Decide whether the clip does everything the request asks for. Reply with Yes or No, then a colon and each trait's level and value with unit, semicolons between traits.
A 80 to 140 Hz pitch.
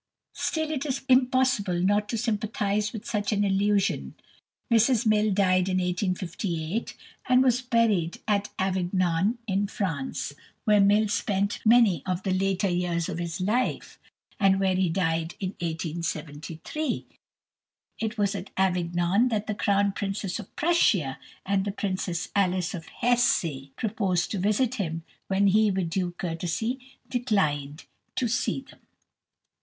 No: high, 195 Hz